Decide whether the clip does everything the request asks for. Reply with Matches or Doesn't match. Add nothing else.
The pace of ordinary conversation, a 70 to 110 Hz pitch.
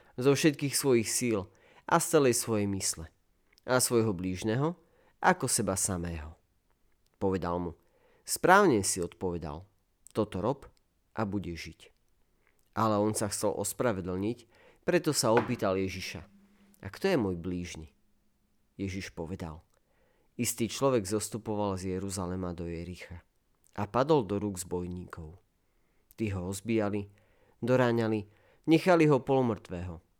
Matches